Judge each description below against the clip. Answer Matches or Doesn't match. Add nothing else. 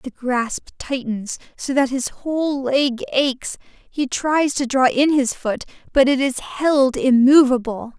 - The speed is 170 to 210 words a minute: Doesn't match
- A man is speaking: Doesn't match